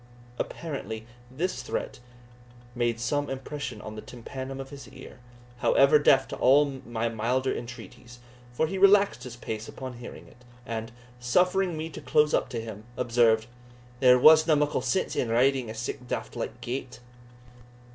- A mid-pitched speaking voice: No, low, 125 Hz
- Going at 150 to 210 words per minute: Yes, average, 160 wpm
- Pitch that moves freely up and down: No, average, 3.5 semitones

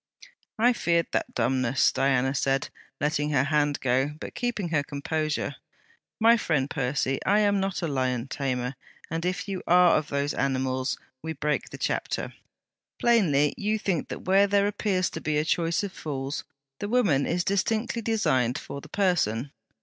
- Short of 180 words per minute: Yes, average, 165 wpm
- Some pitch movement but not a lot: No, wide, 6.2 semitones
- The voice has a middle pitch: Yes, medium, 155 Hz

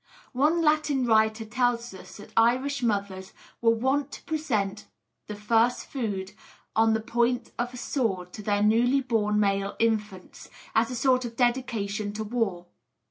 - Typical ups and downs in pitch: Yes, average, 3.1 semitones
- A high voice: Yes, high, 225 Hz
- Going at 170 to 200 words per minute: No, average, 155 wpm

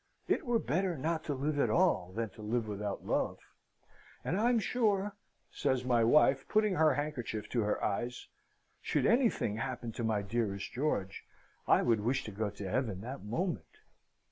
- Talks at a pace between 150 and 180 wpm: Yes, average, 170 wpm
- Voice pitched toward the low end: Yes, low, 125 Hz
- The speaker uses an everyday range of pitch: No, wide, 7.2 semitones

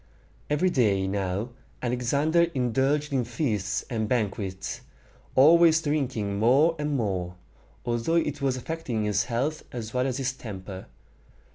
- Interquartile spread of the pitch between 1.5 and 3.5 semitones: No, wide, 5.4 semitones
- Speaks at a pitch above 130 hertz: No, low, 125 Hz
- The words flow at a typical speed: No, slow, 130 wpm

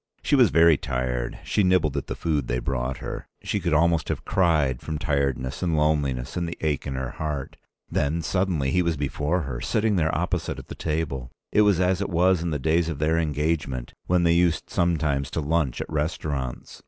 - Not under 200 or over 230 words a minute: Yes, fast, 205 wpm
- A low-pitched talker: Yes, very low, 75 Hz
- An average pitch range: Yes, average, 3.7 semitones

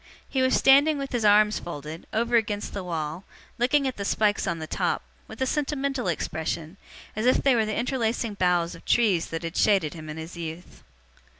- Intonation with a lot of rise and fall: Yes, wide, 6.7 semitones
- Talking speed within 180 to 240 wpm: Yes, average, 200 wpm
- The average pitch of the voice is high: Yes, high, 205 Hz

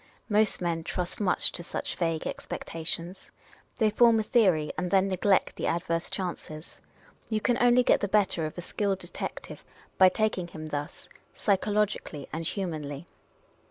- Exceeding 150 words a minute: Yes, average, 160 wpm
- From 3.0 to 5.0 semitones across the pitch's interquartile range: Yes, average, 4.0 semitones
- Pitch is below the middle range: No, medium, 185 Hz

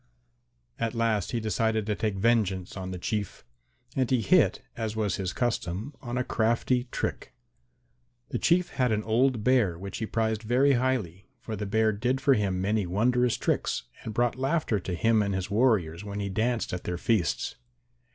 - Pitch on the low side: Yes, low, 110 Hz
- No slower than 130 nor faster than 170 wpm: No, average, 180 wpm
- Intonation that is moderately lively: Yes, average, 3.5 semitones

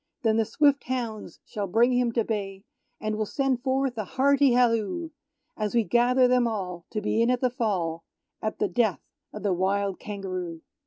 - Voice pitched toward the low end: No, high, 225 Hz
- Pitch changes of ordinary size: Yes, average, 3.9 semitones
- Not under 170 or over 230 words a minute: Yes, average, 190 wpm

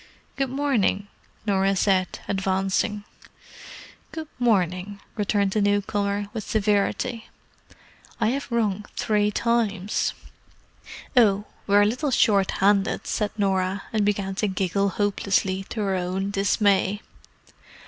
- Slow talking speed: Yes, slow, 105 wpm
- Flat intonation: Yes, narrow, 1.7 semitones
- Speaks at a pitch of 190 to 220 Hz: Yes, high, 205 Hz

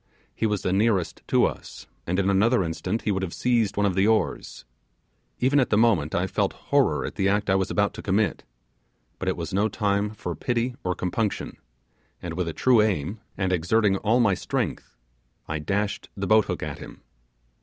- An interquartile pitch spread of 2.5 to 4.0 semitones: Yes, average, 2.9 semitones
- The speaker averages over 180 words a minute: Yes, average, 200 wpm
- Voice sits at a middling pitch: No, low, 100 Hz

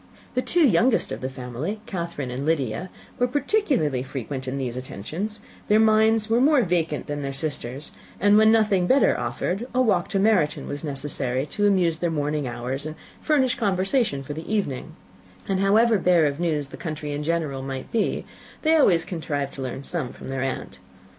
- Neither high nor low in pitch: Yes, medium, 165 Hz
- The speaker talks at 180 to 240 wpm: Yes, average, 185 wpm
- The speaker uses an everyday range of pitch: No, wide, 7.5 semitones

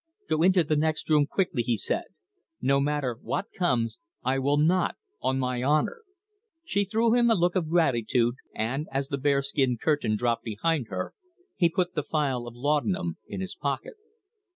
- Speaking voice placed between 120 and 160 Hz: Yes, medium, 140 Hz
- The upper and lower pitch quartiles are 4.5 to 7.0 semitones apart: Yes, average, 5.0 semitones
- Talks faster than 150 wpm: Yes, average, 175 wpm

